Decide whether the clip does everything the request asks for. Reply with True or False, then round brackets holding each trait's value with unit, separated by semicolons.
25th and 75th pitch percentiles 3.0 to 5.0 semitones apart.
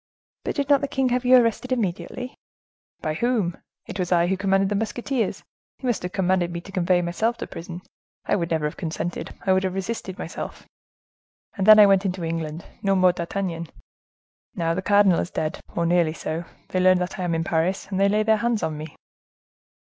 True (3.7 semitones)